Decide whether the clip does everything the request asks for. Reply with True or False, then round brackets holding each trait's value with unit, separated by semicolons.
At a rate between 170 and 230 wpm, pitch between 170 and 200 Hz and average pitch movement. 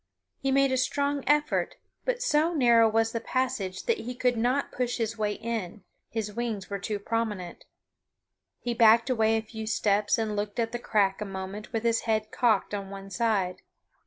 False (190 wpm; 225 Hz; 3.0 semitones)